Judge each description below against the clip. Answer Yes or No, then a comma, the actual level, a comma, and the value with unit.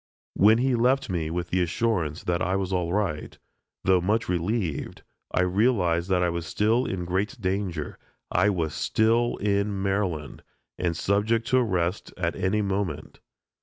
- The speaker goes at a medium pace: Yes, average, 160 wpm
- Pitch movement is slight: No, average, 3.4 semitones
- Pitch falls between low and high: No, very low, 95 Hz